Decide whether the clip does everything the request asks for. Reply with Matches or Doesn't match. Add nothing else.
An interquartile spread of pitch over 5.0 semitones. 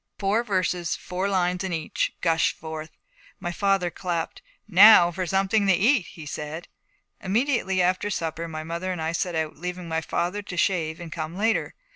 Doesn't match